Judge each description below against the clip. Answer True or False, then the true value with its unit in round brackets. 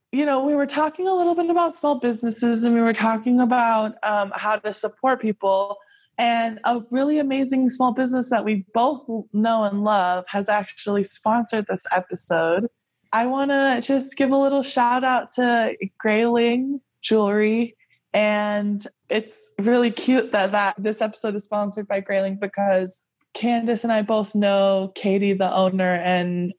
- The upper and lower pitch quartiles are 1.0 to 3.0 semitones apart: False (3.6 semitones)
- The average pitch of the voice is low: False (225 Hz)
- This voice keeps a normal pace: True (160 wpm)